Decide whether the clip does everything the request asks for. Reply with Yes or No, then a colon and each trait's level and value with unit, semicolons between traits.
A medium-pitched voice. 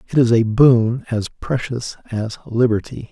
No: low, 115 Hz